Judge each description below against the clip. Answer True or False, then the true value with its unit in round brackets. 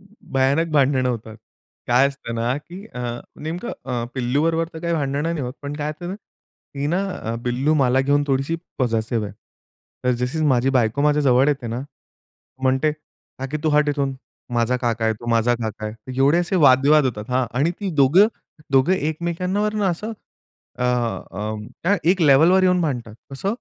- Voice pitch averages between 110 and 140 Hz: True (135 Hz)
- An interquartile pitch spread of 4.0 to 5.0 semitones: True (4.6 semitones)